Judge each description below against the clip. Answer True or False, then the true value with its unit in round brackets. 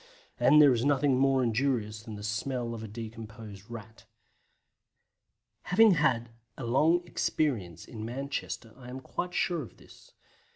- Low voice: True (120 Hz)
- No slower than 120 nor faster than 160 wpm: True (150 wpm)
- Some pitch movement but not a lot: True (4.0 semitones)